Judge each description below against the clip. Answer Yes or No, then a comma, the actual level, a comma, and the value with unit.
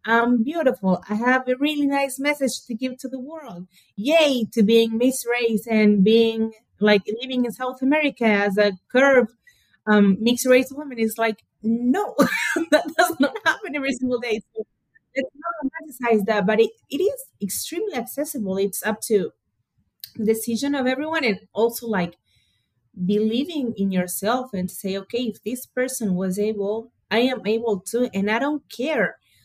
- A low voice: No, high, 235 Hz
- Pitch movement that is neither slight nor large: Yes, average, 3.9 semitones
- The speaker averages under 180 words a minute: Yes, average, 170 wpm